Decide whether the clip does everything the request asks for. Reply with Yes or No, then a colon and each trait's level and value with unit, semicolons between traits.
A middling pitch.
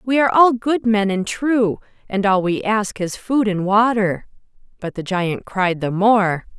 No: high, 205 Hz